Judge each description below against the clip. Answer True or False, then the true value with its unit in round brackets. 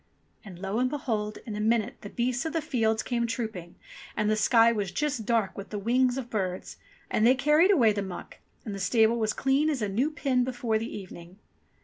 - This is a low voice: False (225 Hz)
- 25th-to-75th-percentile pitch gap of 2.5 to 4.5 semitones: True (3.4 semitones)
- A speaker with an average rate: False (225 wpm)